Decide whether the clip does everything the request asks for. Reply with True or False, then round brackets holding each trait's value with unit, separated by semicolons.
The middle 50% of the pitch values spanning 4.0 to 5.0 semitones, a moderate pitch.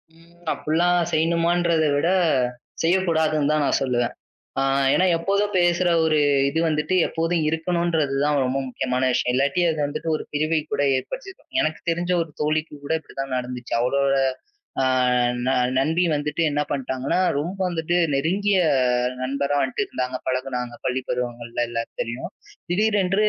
True (4.4 semitones; 155 Hz)